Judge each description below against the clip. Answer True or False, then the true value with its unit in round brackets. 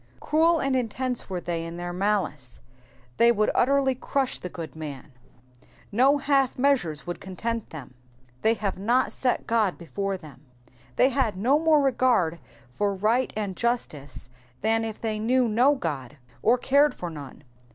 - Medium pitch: False (220 Hz)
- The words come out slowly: False (160 wpm)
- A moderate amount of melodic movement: False (6.8 semitones)